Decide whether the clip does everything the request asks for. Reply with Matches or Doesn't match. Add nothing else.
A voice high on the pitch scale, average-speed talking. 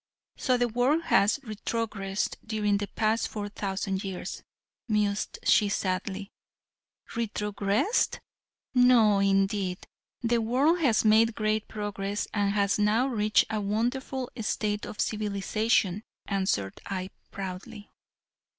Doesn't match